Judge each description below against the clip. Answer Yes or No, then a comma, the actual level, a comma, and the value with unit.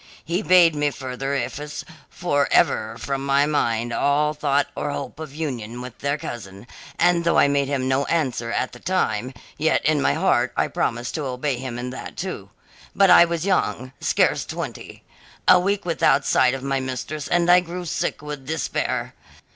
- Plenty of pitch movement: No, average, 3.8 semitones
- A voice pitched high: No, medium, 140 Hz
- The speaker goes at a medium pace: Yes, average, 185 wpm